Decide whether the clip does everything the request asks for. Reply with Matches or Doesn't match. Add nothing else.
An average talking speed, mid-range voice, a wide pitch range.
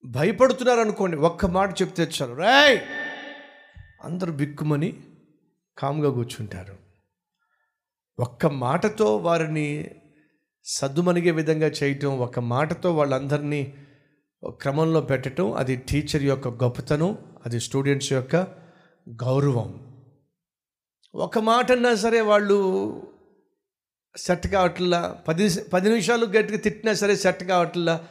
Matches